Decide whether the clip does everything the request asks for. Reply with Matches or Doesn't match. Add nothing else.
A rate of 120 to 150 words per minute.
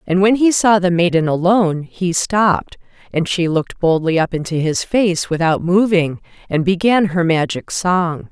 Doesn't match